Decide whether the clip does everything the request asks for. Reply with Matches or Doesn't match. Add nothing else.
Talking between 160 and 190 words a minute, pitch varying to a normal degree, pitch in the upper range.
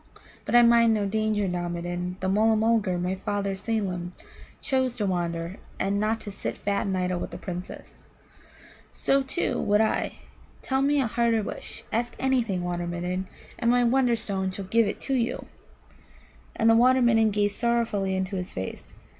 Matches